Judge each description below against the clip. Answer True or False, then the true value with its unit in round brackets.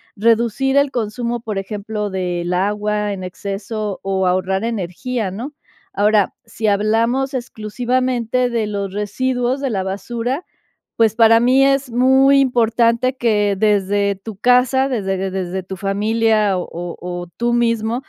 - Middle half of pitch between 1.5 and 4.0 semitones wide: True (3.7 semitones)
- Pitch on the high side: True (220 Hz)